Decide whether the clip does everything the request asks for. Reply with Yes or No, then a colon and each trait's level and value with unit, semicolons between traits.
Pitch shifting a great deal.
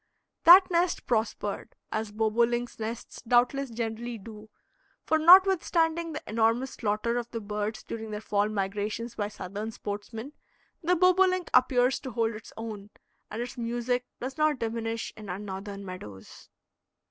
No: average, 3.3 semitones